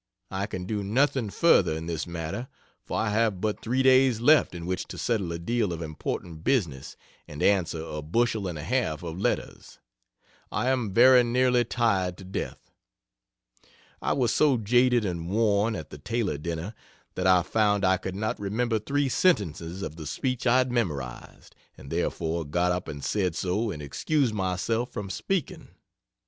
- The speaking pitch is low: Yes, low, 100 Hz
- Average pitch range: No, wide, 5.9 semitones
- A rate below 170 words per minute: No, average, 175 wpm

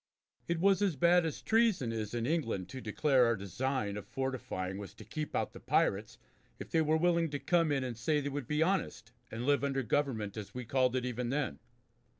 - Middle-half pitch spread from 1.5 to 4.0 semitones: No, average, 5.3 semitones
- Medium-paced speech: No, fast, 215 wpm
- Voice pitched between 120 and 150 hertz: Yes, low, 135 Hz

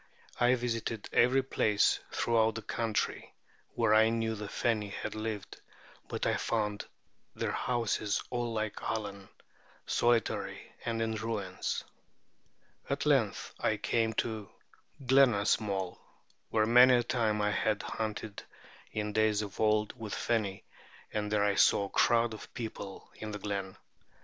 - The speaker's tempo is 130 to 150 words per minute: Yes, average, 140 wpm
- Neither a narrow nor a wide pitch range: No, narrow, 1.8 semitones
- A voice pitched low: Yes, low, 110 Hz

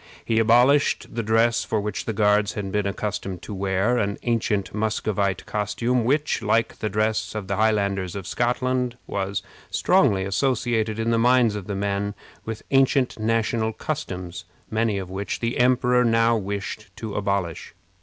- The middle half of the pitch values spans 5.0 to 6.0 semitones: No, average, 2.8 semitones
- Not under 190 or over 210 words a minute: No, average, 155 wpm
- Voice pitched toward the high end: No, low, 110 Hz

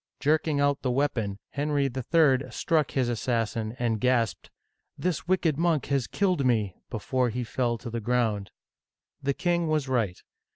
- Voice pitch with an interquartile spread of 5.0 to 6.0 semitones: No, average, 4.3 semitones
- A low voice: Yes, low, 130 Hz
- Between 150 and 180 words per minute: Yes, average, 160 wpm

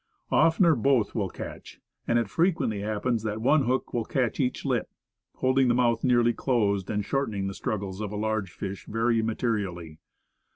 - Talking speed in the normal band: Yes, average, 170 wpm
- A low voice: Yes, low, 115 Hz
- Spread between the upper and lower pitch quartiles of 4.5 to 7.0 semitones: No, average, 3.5 semitones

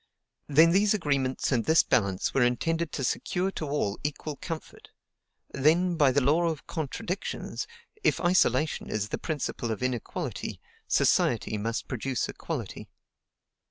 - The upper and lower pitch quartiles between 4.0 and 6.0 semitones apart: Yes, average, 4.8 semitones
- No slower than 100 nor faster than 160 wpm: Yes, slow, 135 wpm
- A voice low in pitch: No, medium, 145 Hz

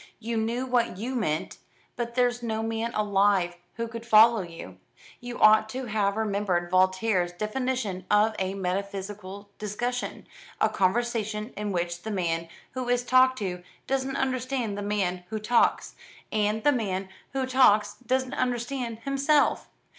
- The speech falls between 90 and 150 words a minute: Yes, average, 145 wpm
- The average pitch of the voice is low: No, high, 220 Hz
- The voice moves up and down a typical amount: Yes, average, 3.8 semitones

